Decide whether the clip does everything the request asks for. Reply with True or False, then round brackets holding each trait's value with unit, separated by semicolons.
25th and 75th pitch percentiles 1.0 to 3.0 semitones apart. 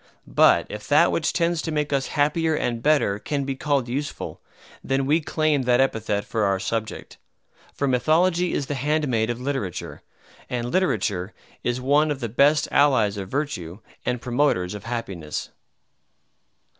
False (4.7 semitones)